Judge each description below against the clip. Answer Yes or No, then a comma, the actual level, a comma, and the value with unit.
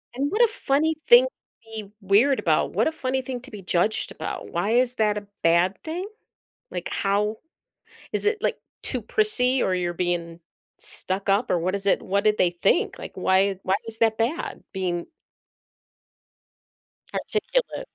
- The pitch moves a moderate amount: No, wide, 6.4 semitones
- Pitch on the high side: Yes, high, 210 Hz